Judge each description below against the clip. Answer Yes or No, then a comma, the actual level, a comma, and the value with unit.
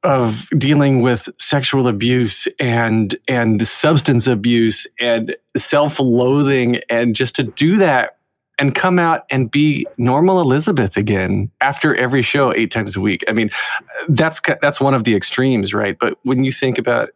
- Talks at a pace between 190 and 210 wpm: No, average, 160 wpm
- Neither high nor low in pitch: No, low, 130 Hz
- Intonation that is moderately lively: Yes, average, 3.6 semitones